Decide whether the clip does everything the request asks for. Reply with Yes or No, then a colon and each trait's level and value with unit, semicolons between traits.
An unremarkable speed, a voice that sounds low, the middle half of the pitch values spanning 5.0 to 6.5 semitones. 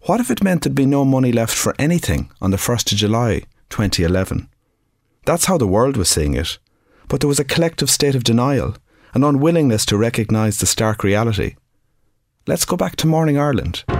Yes: average, 195 wpm; low, 115 Hz; wide, 5.6 semitones